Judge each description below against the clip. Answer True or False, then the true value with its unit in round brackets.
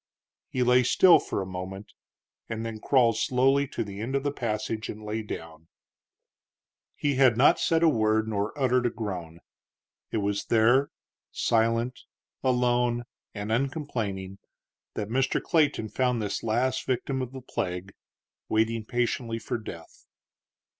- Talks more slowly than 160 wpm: True (145 wpm)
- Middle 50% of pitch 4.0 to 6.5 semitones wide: False (3.3 semitones)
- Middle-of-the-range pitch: False (115 Hz)